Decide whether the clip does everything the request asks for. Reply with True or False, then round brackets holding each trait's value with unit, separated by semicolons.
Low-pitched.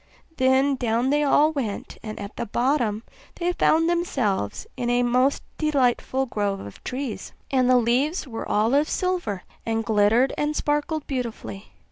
False (255 Hz)